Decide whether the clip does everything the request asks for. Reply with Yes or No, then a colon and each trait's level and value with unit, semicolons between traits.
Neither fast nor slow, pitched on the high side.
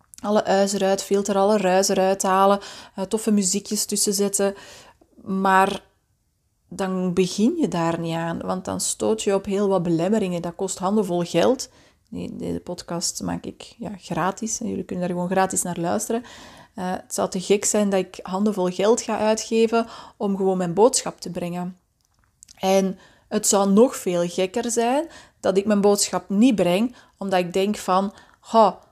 Yes: average, 165 wpm; high, 195 Hz